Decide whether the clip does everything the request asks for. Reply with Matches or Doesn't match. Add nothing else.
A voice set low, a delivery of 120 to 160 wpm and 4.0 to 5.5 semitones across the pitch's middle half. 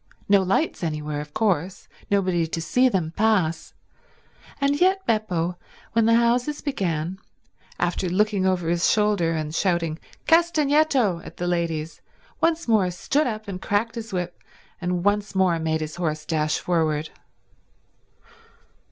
Doesn't match